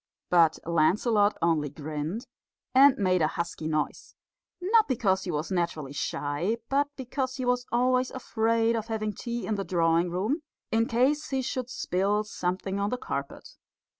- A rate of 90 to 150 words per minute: No, average, 160 wpm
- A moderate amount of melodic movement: No, wide, 6.6 semitones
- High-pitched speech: Yes, high, 210 Hz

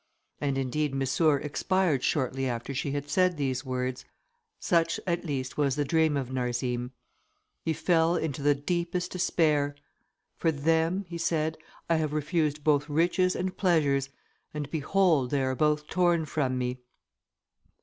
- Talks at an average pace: Yes, average, 150 wpm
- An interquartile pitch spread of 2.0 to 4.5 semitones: Yes, average, 3.5 semitones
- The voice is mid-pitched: Yes, medium, 150 Hz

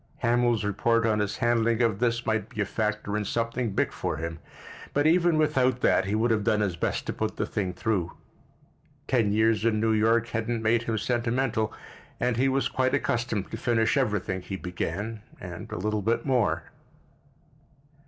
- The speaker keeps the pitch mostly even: Yes, narrow, 2.3 semitones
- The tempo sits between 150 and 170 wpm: No, average, 180 wpm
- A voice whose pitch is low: Yes, low, 115 Hz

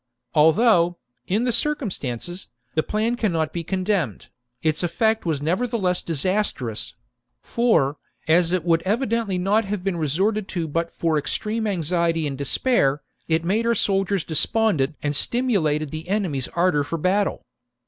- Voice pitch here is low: No, medium, 180 Hz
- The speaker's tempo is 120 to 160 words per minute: Yes, average, 145 wpm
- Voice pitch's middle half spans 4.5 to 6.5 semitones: Yes, average, 5.1 semitones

